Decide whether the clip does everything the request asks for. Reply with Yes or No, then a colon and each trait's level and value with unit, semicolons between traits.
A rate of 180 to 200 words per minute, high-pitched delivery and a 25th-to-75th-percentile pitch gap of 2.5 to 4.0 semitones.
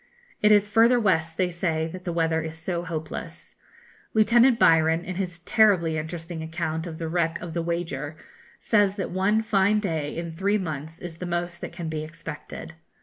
No: average, 185 wpm; medium, 170 Hz; average, 3.0 semitones